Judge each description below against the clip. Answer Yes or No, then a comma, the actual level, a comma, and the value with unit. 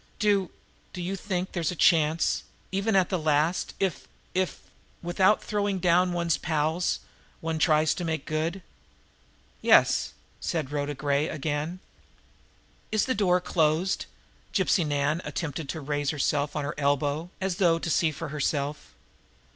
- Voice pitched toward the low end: No, medium, 165 Hz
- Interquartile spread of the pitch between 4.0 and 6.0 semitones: No, average, 3.5 semitones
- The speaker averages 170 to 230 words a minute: No, average, 145 wpm